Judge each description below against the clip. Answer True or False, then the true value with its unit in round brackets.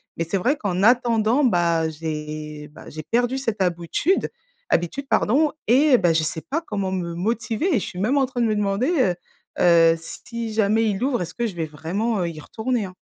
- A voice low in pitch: False (205 Hz)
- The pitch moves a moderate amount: False (6.1 semitones)